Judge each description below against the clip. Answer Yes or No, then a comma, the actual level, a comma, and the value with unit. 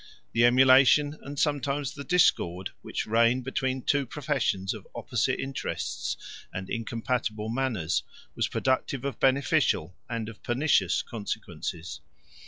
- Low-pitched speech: Yes, low, 125 Hz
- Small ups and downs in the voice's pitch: No, average, 4.2 semitones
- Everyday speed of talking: No, slow, 120 wpm